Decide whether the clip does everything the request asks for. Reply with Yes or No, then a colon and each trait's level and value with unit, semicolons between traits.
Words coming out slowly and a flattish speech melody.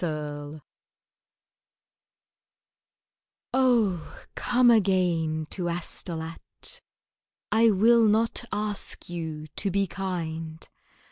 No: slow, 75 wpm; average, 4.9 semitones